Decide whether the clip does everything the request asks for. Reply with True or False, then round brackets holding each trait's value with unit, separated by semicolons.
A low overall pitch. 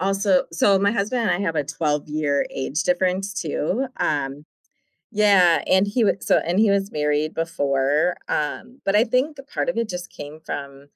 False (180 Hz)